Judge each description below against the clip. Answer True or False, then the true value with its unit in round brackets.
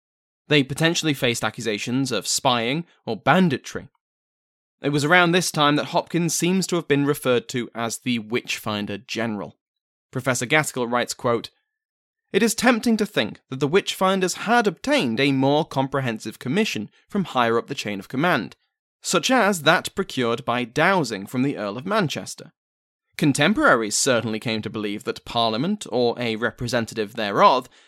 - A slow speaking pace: False (155 wpm)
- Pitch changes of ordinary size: False (7.2 semitones)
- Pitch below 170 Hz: True (135 Hz)